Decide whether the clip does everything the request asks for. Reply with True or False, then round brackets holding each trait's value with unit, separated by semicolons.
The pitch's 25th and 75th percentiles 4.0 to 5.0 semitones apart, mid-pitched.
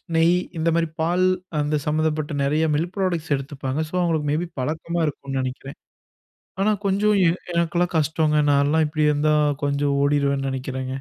False (2.8 semitones; 150 Hz)